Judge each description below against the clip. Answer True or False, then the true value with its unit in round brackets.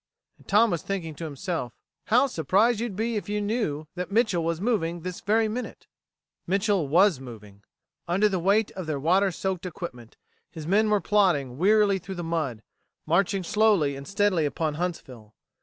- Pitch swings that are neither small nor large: True (4.7 semitones)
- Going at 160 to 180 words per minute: True (175 wpm)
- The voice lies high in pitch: False (180 Hz)